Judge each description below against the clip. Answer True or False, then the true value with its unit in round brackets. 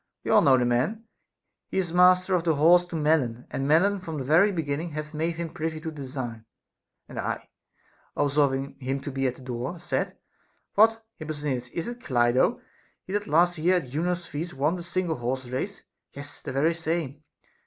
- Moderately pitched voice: True (155 Hz)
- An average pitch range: True (4.5 semitones)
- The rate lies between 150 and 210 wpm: True (195 wpm)